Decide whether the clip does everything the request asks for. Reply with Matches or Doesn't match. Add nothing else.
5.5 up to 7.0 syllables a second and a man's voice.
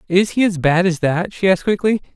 Matches